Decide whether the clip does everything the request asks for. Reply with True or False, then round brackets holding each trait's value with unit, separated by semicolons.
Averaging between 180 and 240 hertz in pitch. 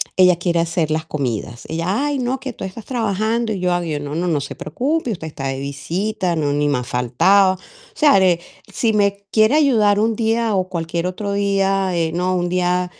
True (185 Hz)